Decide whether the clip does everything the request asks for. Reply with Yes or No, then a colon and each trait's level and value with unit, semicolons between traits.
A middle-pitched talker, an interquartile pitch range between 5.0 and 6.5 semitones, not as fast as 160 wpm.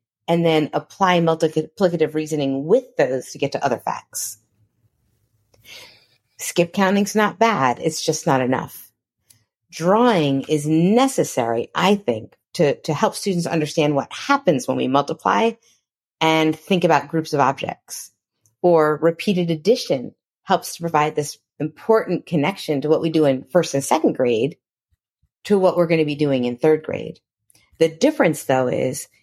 No: medium, 155 Hz; average, 4.2 semitones; average, 150 wpm